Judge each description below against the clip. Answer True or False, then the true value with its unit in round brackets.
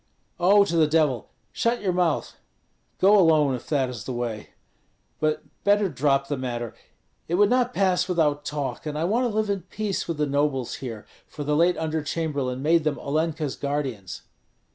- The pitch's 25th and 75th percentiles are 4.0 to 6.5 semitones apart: True (4.6 semitones)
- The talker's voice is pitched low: False (155 Hz)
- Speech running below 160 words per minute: False (185 wpm)